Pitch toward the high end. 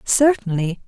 Yes: high, 215 Hz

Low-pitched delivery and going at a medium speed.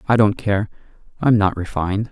Yes: low, 105 Hz; average, 170 wpm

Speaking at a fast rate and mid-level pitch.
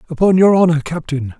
No: average, 170 wpm; medium, 160 Hz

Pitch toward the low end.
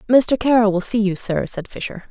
No: high, 215 Hz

